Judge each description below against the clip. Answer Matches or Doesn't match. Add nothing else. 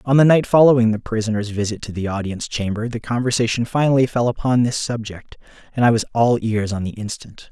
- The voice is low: Matches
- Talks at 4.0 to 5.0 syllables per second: Doesn't match